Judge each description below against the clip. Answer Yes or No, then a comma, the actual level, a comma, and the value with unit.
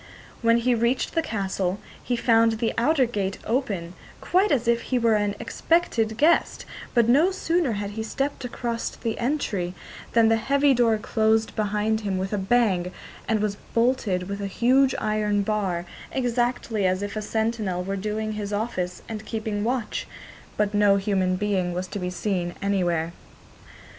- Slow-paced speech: No, average, 170 wpm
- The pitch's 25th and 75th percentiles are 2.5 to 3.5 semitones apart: Yes, average, 3.0 semitones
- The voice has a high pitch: Yes, high, 215 Hz